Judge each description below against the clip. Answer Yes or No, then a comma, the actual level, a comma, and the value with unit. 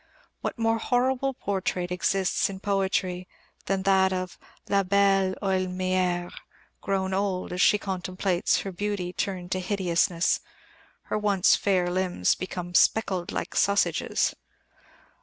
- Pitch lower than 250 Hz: Yes, high, 190 Hz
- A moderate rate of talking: No, slow, 120 wpm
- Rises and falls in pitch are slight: Yes, narrow, 1.7 semitones